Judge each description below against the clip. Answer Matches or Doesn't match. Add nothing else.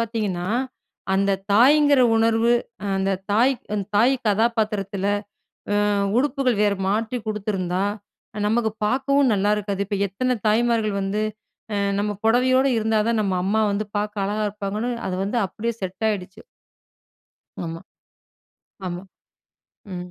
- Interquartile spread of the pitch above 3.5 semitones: Doesn't match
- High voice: Matches